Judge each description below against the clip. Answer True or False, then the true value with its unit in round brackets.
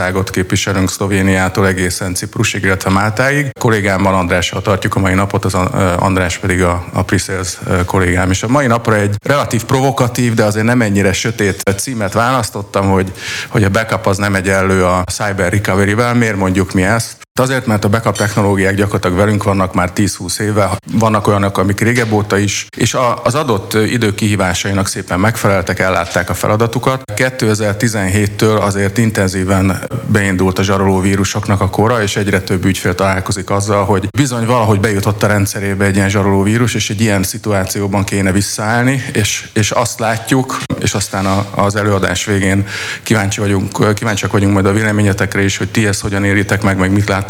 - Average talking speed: False (170 wpm)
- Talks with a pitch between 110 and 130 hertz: False (100 Hz)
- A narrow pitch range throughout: True (2.2 semitones)